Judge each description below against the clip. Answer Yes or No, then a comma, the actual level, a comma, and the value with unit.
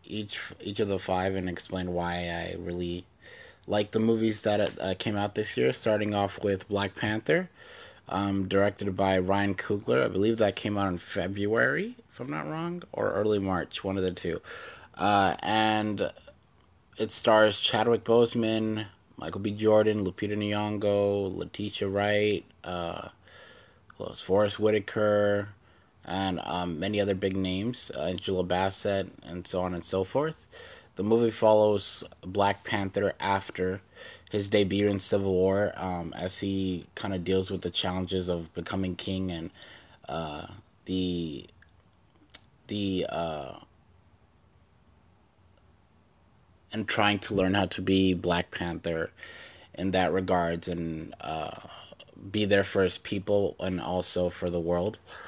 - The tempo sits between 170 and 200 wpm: No, average, 140 wpm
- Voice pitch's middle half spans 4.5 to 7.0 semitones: No, narrow, 2.4 semitones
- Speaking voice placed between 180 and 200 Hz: No, very low, 95 Hz